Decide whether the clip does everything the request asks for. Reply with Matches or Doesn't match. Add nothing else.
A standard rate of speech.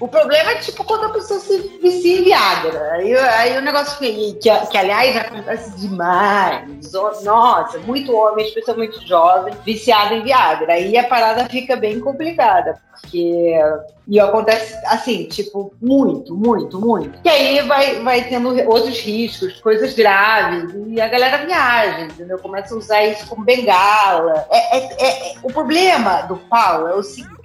Matches